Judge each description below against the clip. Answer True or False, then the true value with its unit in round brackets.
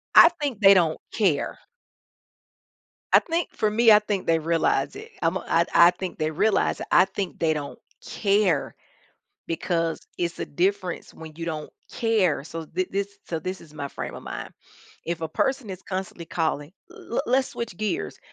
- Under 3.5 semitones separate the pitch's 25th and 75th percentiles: False (4.2 semitones)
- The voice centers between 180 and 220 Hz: True (185 Hz)